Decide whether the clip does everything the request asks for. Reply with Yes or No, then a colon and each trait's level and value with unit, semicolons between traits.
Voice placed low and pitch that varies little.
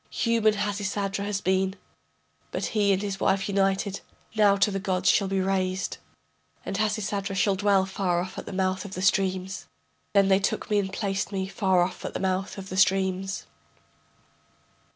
No: high, 195 Hz; narrow, 1.0 semitones